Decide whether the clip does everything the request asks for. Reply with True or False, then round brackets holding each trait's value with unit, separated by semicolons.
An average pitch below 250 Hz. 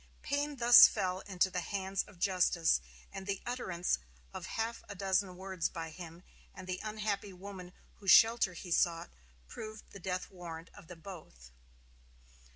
True (190 Hz)